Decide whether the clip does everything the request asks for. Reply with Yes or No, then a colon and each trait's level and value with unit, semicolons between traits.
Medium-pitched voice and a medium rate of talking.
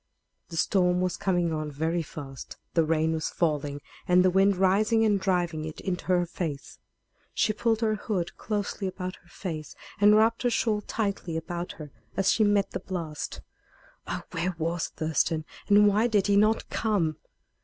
Yes: medium, 180 Hz; average, 175 wpm